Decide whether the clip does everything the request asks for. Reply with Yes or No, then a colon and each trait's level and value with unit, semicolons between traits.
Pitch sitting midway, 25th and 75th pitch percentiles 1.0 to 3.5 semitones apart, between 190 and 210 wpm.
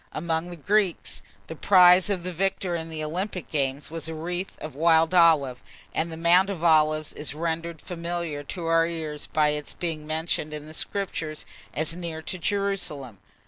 No: medium, 165 Hz; narrow, 2.4 semitones; average, 180 wpm